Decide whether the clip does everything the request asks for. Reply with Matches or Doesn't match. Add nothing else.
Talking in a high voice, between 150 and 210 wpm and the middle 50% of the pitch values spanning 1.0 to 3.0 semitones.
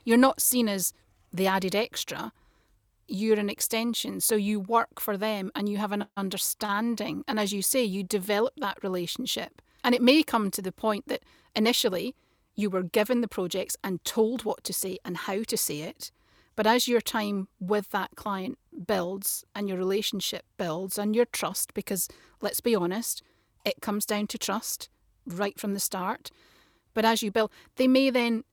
Matches